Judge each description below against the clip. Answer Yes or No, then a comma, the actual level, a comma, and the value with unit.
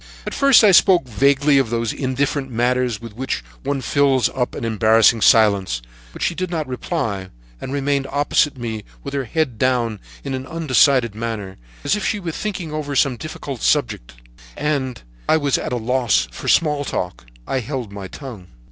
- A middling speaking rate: Yes, average, 185 wpm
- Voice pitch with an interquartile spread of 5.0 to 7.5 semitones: No, average, 4.0 semitones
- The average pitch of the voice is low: Yes, low, 130 Hz